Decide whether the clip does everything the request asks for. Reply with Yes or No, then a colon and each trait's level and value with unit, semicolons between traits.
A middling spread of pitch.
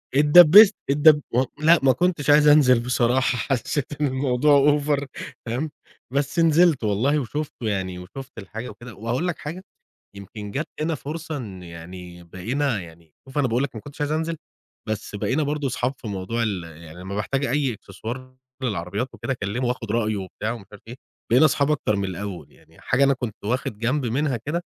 No: wide, 5.9 semitones